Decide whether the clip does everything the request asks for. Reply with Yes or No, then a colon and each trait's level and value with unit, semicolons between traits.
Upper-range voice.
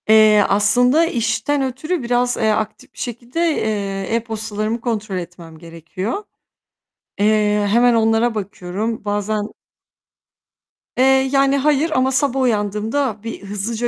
Yes: high, 225 Hz